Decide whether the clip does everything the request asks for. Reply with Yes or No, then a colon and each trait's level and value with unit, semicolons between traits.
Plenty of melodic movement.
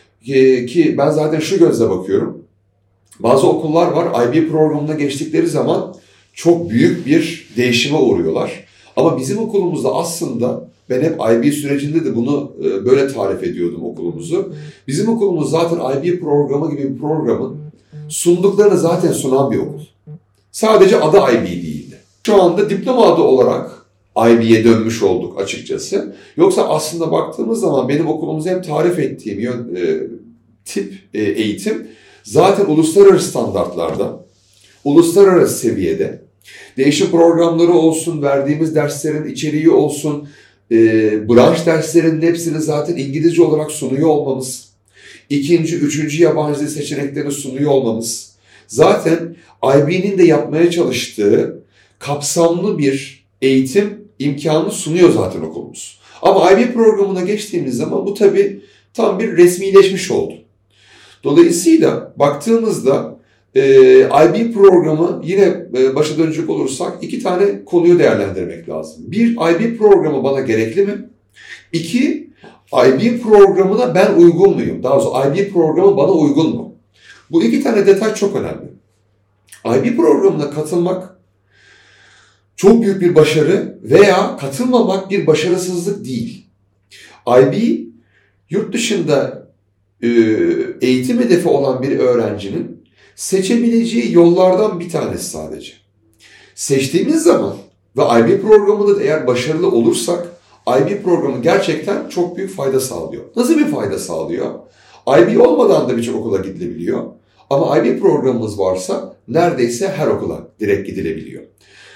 Yes: wide, 7.0 semitones